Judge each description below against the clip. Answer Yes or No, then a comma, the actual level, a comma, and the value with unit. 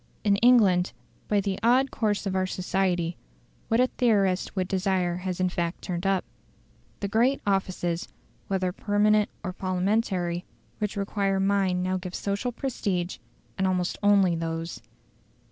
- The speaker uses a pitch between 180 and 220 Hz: Yes, high, 190 Hz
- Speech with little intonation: Yes, narrow, 2.2 semitones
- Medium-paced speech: Yes, average, 145 wpm